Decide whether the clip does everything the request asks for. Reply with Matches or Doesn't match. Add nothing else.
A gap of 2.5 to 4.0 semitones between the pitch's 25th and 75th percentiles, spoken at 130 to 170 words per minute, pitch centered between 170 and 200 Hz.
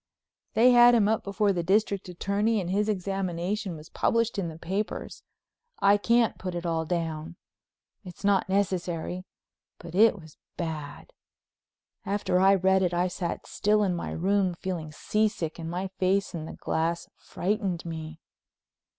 Matches